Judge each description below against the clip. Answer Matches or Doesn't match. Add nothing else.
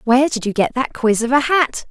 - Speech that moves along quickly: Matches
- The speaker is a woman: Matches